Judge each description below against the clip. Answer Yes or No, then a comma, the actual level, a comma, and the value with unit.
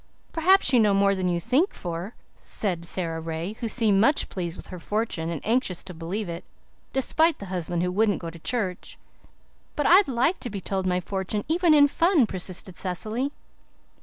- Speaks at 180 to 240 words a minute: Yes, average, 190 wpm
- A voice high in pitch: Yes, high, 200 Hz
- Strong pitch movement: Yes, wide, 6.0 semitones